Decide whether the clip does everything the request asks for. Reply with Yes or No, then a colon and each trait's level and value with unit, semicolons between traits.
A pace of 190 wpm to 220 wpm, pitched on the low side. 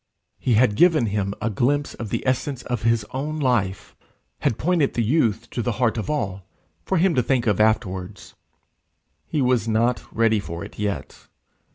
No: average, 180 wpm; low, 115 Hz